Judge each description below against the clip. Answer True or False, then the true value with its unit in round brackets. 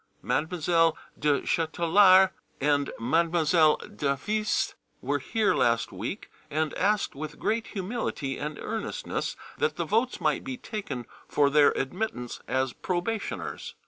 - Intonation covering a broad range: True (6.4 semitones)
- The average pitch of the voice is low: False (165 Hz)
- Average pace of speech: False (120 wpm)